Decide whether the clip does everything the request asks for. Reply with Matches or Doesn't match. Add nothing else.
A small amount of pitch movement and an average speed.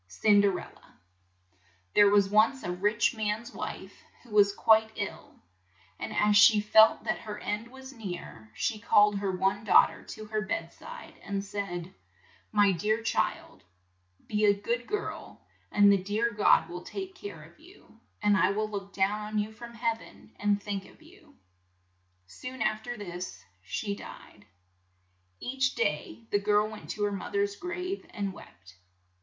Matches